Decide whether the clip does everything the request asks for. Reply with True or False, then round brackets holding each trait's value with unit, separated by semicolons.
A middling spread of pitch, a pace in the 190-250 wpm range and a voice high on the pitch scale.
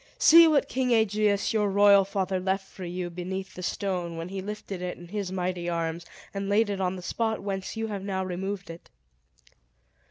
False (2.1 semitones; 195 wpm; 195 Hz)